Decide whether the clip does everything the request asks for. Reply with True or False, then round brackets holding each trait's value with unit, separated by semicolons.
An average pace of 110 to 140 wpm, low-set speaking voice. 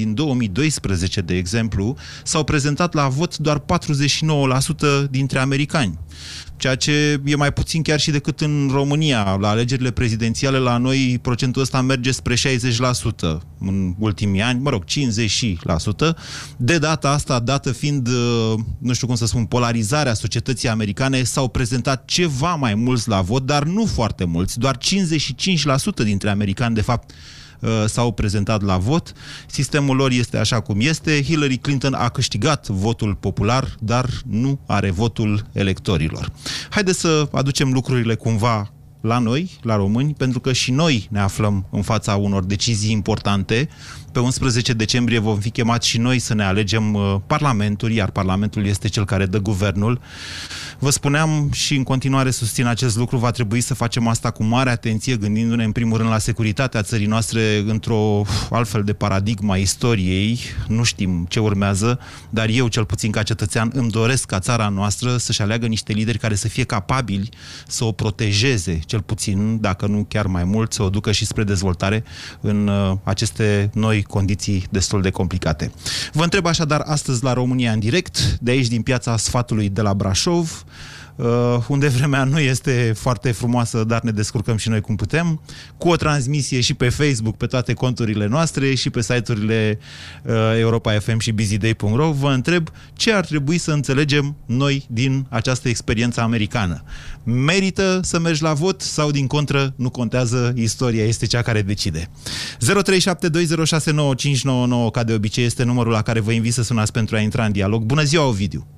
False (165 wpm; 120 Hz)